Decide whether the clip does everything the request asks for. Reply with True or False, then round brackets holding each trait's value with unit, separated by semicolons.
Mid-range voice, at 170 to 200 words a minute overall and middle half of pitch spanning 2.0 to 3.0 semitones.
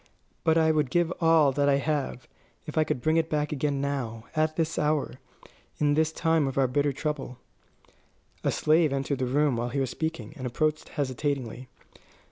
True (145 Hz; 185 wpm; 2.7 semitones)